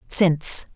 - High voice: No, medium, 165 Hz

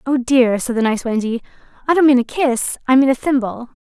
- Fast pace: Yes, fast, 235 wpm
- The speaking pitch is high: Yes, very high, 255 Hz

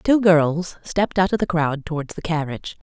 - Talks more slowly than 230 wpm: Yes, fast, 205 wpm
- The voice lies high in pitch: No, medium, 170 Hz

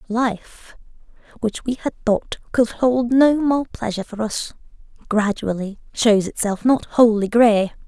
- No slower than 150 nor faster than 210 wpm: No, slow, 135 wpm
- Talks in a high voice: Yes, high, 225 Hz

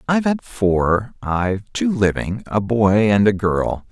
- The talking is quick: No, average, 155 wpm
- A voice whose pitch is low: Yes, low, 110 Hz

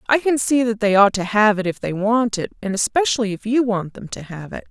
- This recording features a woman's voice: Yes, female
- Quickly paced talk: Yes, fast, 280 wpm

